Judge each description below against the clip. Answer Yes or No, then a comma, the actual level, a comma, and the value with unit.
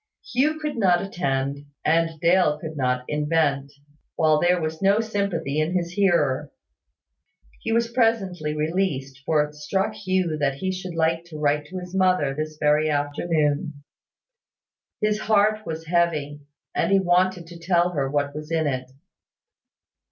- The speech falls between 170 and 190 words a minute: No, average, 150 wpm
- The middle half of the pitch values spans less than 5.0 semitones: Yes, average, 4.0 semitones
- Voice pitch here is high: No, medium, 165 Hz